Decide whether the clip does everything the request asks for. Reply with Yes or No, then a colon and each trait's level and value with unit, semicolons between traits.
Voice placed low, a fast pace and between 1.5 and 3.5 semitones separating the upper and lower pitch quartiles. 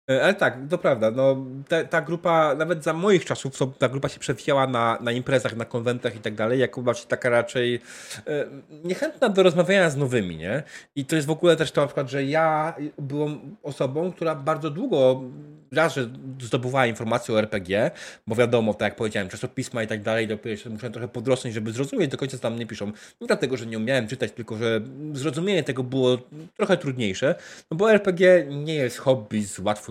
No: low, 130 Hz; fast, 200 wpm; average, 5.0 semitones